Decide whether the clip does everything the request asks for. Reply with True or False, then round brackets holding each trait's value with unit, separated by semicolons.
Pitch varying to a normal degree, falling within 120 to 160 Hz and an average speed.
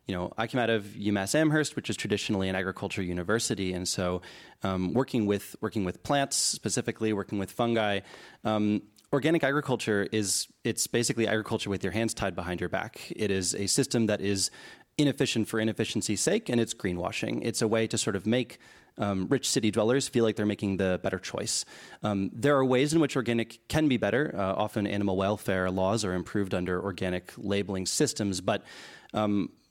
False (3.2 semitones; 105 Hz; 190 wpm)